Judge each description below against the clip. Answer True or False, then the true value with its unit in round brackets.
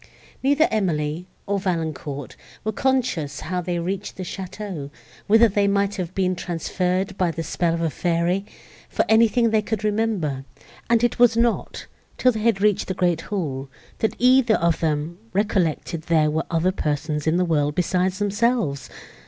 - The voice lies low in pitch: False (185 Hz)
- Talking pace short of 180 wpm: True (165 wpm)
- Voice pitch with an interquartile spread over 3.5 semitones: True (4.5 semitones)